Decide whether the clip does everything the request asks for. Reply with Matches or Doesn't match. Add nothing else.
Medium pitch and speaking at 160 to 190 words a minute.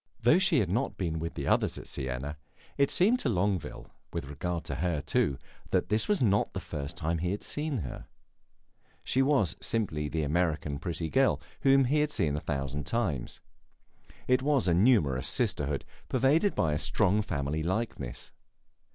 Doesn't match